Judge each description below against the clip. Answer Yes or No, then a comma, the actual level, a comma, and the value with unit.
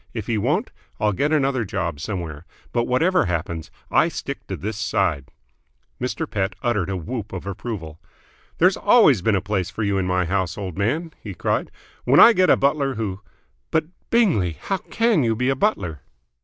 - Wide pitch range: Yes, wide, 7.0 semitones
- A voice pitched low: Yes, low, 105 Hz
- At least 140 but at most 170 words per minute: No, average, 190 wpm